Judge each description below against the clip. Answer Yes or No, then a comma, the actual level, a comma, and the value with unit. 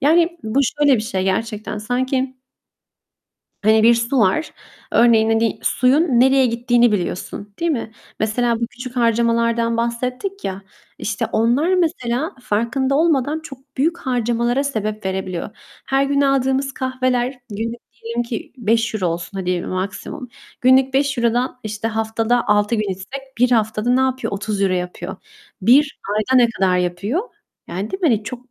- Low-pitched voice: No, high, 235 Hz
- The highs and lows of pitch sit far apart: No, average, 3.6 semitones